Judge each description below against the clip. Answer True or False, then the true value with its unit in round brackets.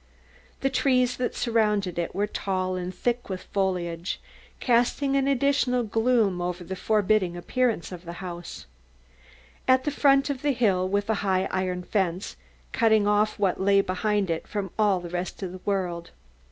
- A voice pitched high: True (200 Hz)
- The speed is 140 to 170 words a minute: True (165 wpm)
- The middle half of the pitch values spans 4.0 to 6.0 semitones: True (4.6 semitones)